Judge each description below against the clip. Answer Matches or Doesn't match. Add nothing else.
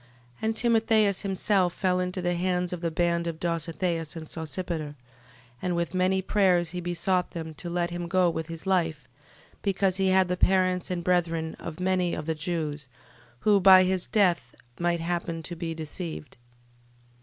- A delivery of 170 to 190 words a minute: Matches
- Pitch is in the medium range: Matches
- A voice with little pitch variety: Matches